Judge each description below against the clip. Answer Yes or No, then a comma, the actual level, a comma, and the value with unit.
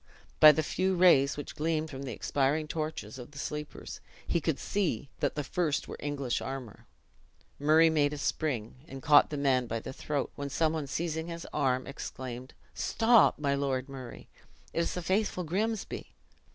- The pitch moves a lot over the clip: No, average, 3.1 semitones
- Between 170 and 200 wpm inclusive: Yes, average, 180 wpm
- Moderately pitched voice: Yes, medium, 145 Hz